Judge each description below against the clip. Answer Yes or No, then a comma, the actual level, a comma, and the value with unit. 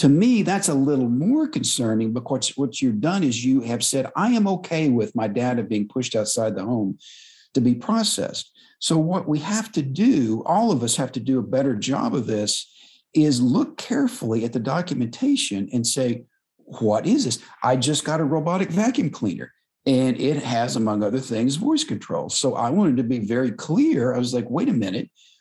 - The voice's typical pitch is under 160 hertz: Yes, low, 135 Hz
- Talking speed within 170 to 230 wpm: Yes, average, 200 wpm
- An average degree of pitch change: No, wide, 7.7 semitones